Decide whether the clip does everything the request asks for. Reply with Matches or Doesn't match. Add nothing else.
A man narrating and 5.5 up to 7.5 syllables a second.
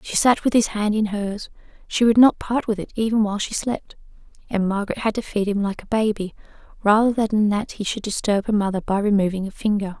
Doesn't match